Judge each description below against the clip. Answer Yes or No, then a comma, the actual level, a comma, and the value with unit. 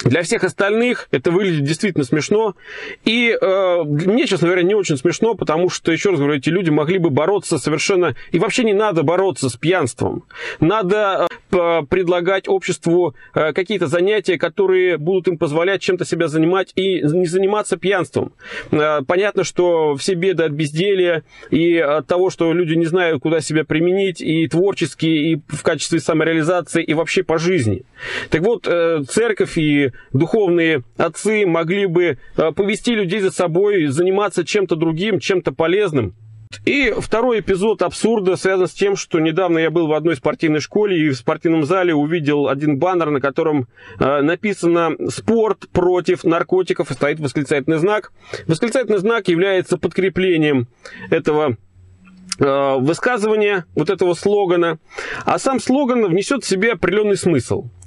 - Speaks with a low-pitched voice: No, medium, 175 Hz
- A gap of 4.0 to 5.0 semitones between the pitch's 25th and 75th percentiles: No, average, 3.6 semitones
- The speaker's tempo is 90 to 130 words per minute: No, average, 145 wpm